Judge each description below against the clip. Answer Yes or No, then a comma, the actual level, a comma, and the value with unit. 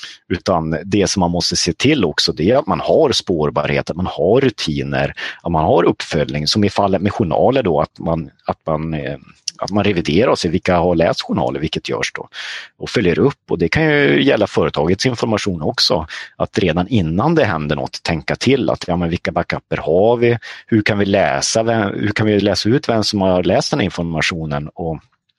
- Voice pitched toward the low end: Yes, very low, 90 Hz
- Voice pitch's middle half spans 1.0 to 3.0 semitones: No, average, 4.4 semitones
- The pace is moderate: No, fast, 210 wpm